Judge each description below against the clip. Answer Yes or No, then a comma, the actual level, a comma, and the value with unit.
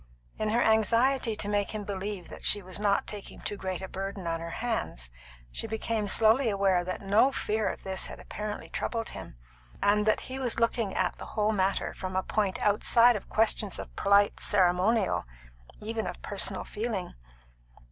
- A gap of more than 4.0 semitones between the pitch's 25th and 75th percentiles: No, narrow, 2.5 semitones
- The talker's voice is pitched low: No, high, 205 Hz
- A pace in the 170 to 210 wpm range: Yes, average, 180 wpm